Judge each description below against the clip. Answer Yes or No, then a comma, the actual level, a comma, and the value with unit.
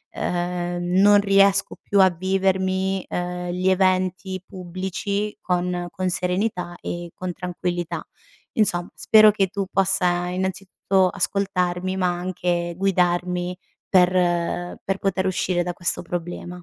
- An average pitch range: No, narrow, 1.4 semitones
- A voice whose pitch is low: No, medium, 185 Hz